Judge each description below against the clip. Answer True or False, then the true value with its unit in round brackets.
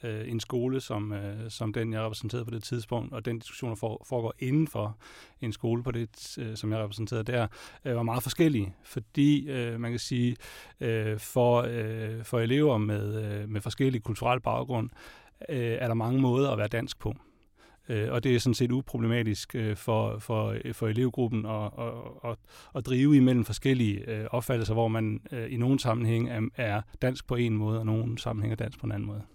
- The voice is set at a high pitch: False (115 Hz)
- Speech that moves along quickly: False (175 wpm)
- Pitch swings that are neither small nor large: False (2.1 semitones)